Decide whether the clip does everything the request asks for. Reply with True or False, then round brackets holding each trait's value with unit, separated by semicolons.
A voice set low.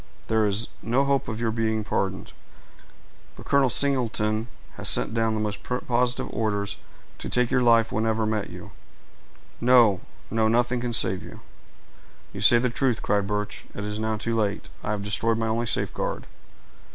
True (110 Hz)